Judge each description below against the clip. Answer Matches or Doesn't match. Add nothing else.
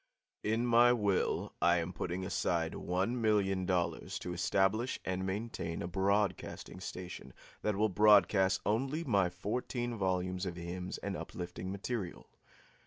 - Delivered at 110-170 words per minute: Matches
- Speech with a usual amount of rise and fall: Matches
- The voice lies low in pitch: Matches